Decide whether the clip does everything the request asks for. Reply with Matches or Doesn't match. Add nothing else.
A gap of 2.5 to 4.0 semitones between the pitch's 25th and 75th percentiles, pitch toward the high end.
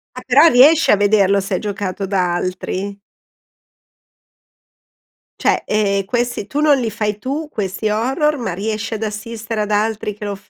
Matches